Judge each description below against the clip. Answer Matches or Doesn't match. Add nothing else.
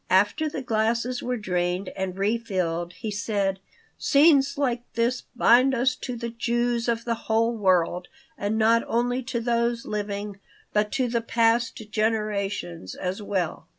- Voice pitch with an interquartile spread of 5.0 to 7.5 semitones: Doesn't match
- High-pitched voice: Matches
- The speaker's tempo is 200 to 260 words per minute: Doesn't match